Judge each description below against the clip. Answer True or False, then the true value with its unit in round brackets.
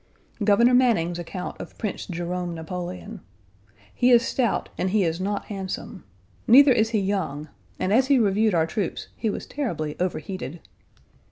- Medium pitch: False (195 Hz)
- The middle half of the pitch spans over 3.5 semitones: True (4.3 semitones)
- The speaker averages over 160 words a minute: False (155 wpm)